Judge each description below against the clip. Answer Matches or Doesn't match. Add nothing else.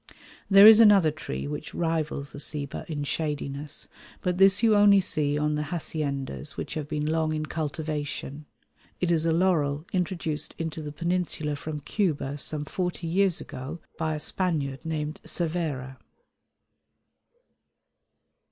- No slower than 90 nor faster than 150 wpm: Matches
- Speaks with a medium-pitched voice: Matches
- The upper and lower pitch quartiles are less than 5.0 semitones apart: Matches